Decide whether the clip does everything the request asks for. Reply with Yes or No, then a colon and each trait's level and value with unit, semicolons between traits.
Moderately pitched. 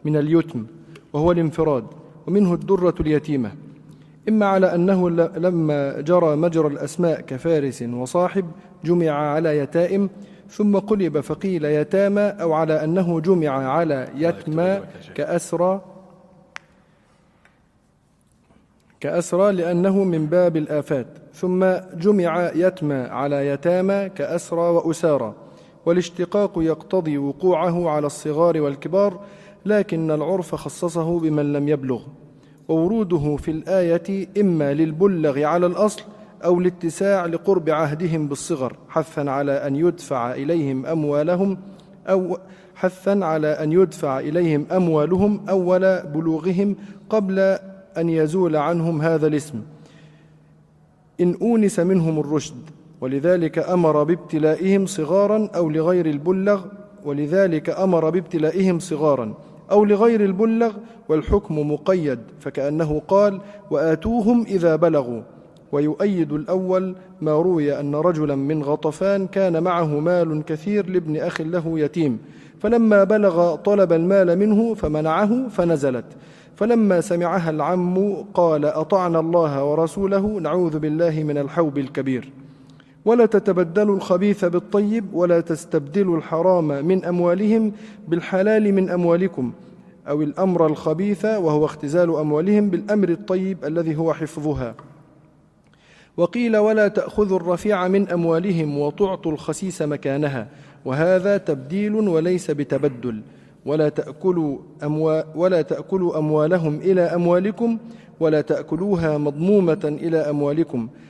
Yes: medium, 170 Hz